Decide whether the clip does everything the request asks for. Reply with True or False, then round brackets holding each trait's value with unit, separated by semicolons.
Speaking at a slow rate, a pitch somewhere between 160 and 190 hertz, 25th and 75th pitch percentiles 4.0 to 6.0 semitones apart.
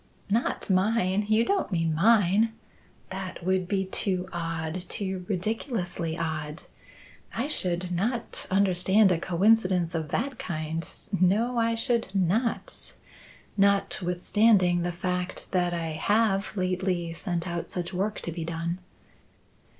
False (125 wpm; 185 Hz; 3.3 semitones)